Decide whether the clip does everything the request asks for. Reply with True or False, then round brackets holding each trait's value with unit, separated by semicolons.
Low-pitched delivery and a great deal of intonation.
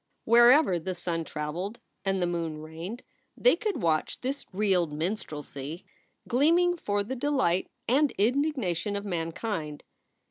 False (195 Hz; 7.0 semitones)